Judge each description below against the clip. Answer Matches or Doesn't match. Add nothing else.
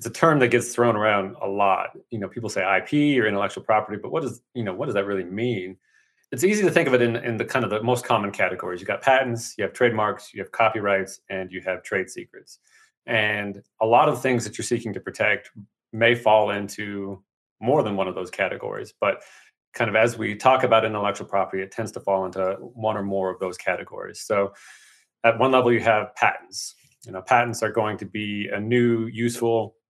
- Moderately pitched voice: Doesn't match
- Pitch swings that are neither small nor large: Matches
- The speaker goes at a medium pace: Doesn't match